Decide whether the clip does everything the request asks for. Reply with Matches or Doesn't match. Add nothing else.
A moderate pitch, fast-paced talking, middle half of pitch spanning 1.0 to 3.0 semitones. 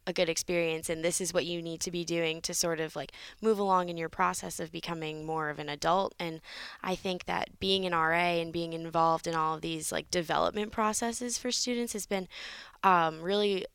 Matches